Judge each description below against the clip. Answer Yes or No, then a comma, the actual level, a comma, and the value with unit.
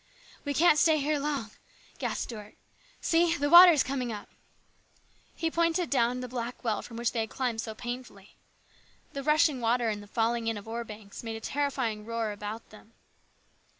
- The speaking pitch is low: No, high, 240 Hz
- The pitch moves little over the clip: No, average, 4.5 semitones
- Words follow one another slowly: No, average, 195 wpm